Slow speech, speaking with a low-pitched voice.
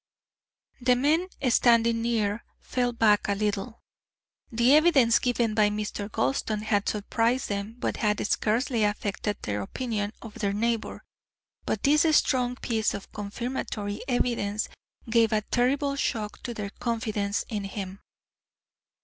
No: slow, 130 wpm; high, 225 Hz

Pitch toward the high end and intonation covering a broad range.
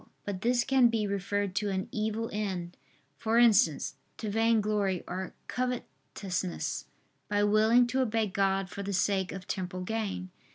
No: high, 205 Hz; average, 2.9 semitones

